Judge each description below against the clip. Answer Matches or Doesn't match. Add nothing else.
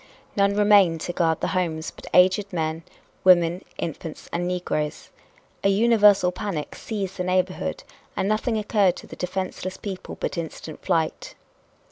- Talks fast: Doesn't match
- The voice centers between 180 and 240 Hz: Matches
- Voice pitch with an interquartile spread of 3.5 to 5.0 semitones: Doesn't match